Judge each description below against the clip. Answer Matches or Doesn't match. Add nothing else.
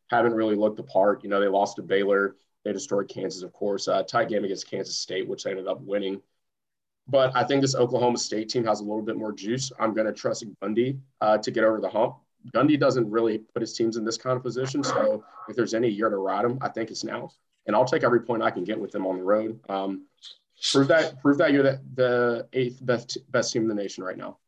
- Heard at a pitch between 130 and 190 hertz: Doesn't match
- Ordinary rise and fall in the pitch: Matches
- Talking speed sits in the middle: Doesn't match